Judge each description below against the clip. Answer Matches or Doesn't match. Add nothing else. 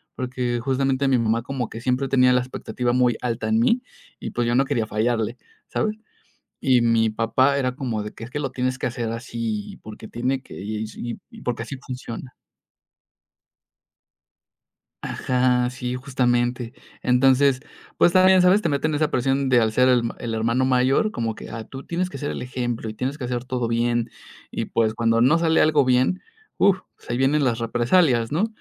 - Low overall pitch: Matches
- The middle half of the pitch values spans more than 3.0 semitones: Doesn't match